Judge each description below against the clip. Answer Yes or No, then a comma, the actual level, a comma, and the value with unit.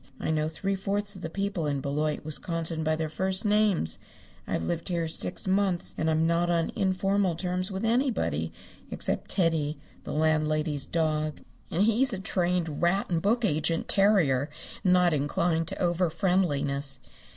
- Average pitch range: Yes, average, 3.6 semitones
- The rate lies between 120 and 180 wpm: Yes, average, 160 wpm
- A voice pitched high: No, medium, 170 Hz